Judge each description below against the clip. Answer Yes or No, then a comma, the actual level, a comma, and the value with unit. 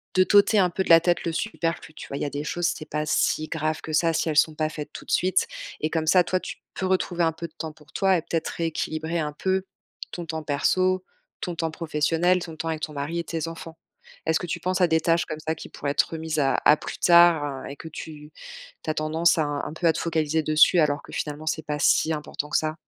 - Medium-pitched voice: Yes, medium, 160 Hz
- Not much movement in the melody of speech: Yes, narrow, 1.9 semitones